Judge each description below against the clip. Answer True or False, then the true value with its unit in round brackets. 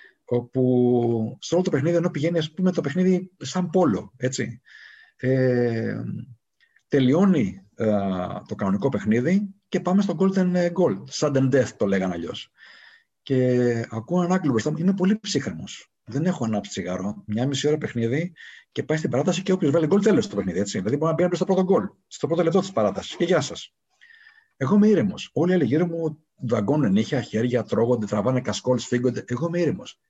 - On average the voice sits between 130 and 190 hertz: True (140 Hz)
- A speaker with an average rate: False (180 wpm)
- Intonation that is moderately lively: False (7.6 semitones)